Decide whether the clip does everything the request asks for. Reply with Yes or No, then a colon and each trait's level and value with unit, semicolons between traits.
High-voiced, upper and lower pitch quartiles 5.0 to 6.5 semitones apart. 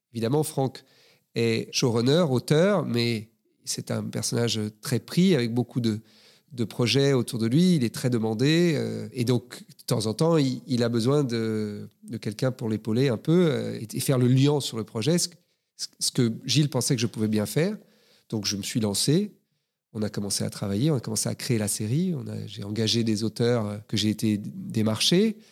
No: low, 120 Hz; wide, 5.5 semitones